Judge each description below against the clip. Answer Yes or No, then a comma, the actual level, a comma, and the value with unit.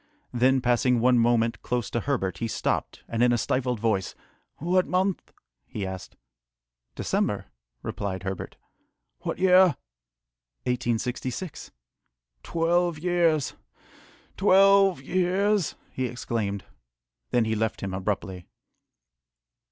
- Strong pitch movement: Yes, wide, 7.7 semitones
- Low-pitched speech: Yes, low, 125 Hz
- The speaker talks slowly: Yes, slow, 105 wpm